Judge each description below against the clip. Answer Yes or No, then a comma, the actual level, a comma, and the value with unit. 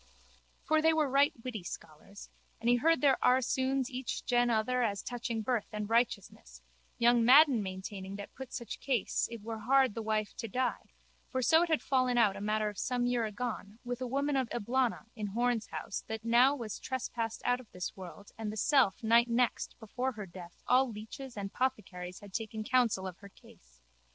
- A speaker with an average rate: Yes, average, 195 wpm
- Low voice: No, high, 235 Hz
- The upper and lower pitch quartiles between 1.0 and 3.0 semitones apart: No, average, 3.5 semitones